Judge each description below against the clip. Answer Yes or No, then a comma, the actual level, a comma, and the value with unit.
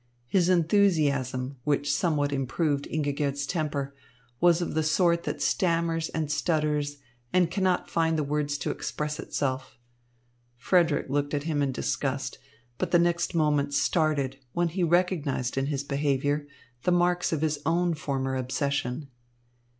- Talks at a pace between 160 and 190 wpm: No, average, 140 wpm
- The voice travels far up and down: No, average, 3.1 semitones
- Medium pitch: Yes, medium, 150 Hz